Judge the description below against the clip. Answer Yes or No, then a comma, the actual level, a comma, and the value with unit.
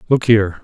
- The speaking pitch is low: Yes, low, 105 Hz